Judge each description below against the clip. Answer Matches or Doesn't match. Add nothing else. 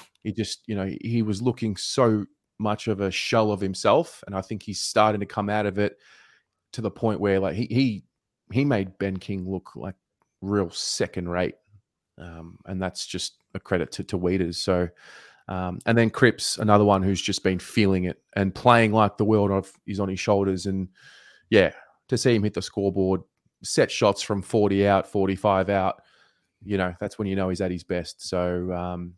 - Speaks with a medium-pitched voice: Doesn't match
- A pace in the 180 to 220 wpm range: Matches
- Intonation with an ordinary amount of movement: Doesn't match